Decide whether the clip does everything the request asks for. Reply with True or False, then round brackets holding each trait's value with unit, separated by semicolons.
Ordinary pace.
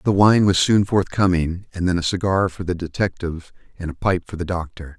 False (215 wpm)